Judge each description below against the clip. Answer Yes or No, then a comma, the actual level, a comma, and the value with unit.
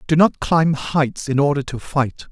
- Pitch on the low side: No, medium, 145 Hz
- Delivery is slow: No, fast, 205 wpm